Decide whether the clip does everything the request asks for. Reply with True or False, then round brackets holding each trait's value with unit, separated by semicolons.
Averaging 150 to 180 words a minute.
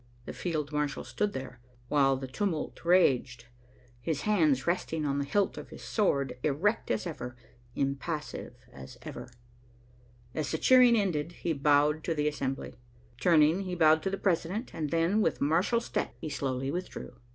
True (165 wpm)